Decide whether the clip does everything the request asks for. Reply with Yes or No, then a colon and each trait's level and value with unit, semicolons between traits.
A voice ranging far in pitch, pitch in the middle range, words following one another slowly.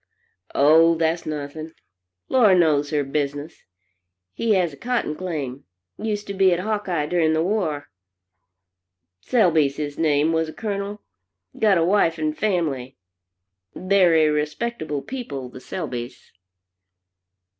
No: average, 4.7 semitones; medium, 160 Hz; slow, 125 wpm